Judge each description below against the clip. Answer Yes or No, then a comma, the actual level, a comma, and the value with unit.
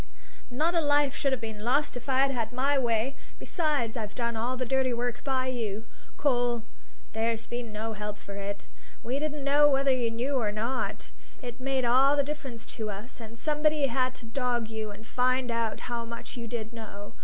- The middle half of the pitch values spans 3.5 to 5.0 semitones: No, average, 3.1 semitones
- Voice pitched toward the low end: No, high, 245 Hz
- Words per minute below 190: No, average, 200 wpm